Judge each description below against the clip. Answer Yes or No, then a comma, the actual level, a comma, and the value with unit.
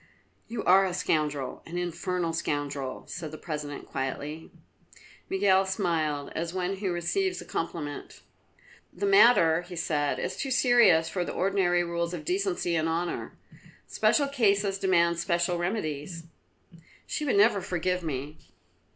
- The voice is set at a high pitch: No, medium, 175 Hz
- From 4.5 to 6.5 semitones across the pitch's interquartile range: No, average, 3.2 semitones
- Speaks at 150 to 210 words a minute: No, average, 140 wpm